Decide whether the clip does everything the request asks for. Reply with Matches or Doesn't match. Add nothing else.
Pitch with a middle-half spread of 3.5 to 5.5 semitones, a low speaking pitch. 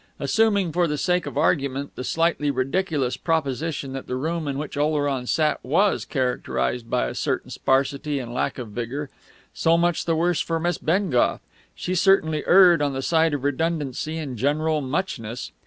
Doesn't match